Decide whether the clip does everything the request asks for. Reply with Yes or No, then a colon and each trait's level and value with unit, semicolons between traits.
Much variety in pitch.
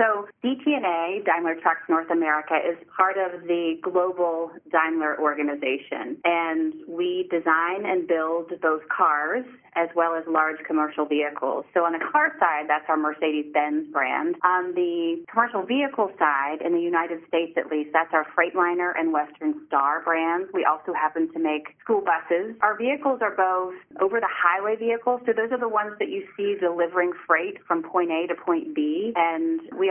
Yes: wide, 5.8 semitones